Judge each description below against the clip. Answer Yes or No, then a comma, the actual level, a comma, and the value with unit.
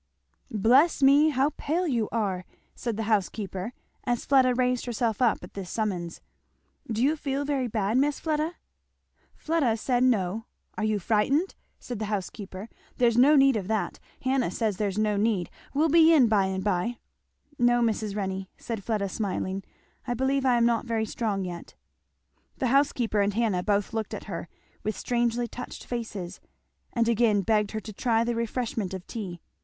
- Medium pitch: No, high, 225 Hz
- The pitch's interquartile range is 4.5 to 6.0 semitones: No, average, 3.7 semitones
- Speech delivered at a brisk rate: No, average, 170 wpm